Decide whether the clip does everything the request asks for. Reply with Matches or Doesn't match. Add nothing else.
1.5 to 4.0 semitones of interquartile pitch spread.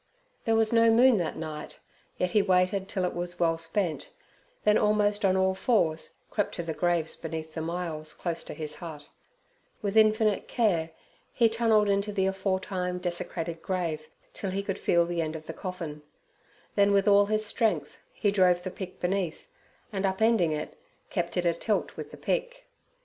Matches